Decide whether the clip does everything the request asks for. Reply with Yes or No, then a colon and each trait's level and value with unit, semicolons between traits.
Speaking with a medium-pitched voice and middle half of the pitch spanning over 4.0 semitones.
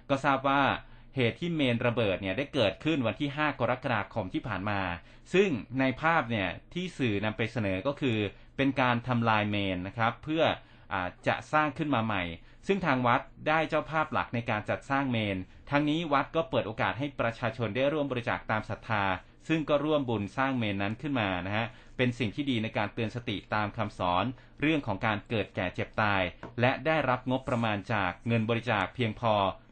No: low, 120 Hz; average, 4.6 semitones